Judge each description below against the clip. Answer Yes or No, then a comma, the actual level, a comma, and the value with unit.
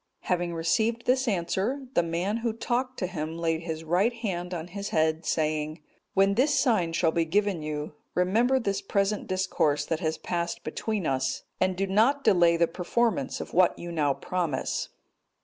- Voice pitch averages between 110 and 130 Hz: No, medium, 180 Hz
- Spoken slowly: No, average, 175 wpm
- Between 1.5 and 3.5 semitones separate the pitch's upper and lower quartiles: No, average, 4.7 semitones